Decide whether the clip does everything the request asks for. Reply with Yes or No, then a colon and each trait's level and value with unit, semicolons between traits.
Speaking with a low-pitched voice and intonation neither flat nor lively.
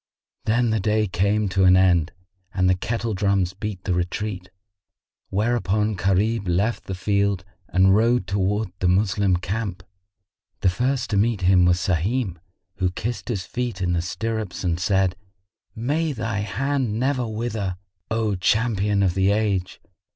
Yes: low, 100 Hz; average, 3.2 semitones